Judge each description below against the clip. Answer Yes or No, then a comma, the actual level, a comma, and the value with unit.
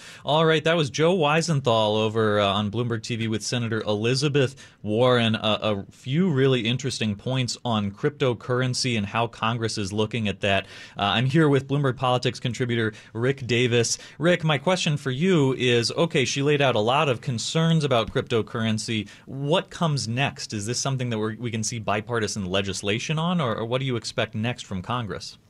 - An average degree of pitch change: Yes, average, 4.0 semitones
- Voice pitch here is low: Yes, low, 120 Hz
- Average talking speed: Yes, average, 180 wpm